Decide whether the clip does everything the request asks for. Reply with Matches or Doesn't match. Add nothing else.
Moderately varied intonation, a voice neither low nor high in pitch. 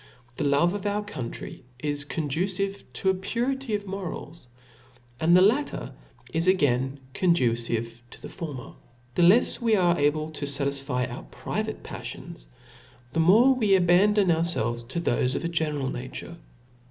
Doesn't match